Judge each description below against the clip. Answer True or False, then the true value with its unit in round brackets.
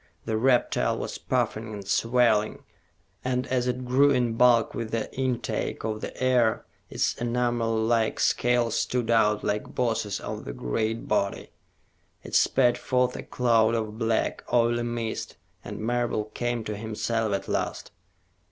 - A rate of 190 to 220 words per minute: False (150 wpm)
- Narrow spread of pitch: True (1.9 semitones)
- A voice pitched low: True (115 Hz)